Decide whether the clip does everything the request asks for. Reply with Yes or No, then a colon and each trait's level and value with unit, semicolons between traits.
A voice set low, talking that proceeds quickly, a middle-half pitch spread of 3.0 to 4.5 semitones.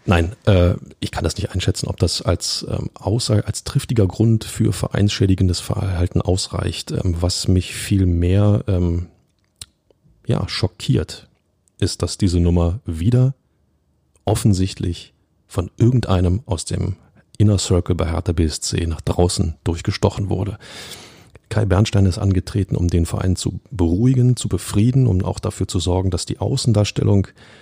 No: very low, 95 Hz; average, 130 wpm; average, 3.4 semitones